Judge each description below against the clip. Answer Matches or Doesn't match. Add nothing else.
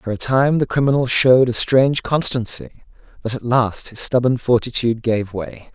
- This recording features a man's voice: Matches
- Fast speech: Doesn't match